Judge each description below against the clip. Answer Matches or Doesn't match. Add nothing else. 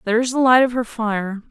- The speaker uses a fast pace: Matches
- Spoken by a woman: Matches